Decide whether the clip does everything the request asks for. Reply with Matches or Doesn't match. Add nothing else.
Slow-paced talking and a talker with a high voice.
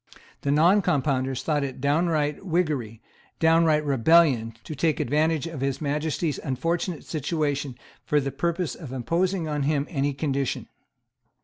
Doesn't match